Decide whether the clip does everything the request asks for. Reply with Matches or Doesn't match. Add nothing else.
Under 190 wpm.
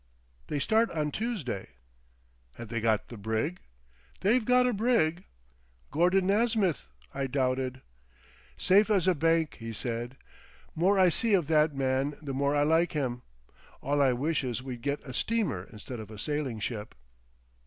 Matches